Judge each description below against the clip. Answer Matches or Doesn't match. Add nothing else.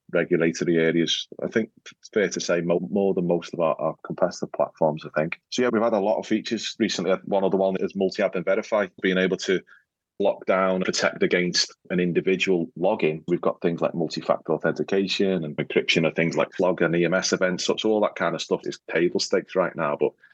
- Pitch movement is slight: Matches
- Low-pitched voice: Matches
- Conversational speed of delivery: Doesn't match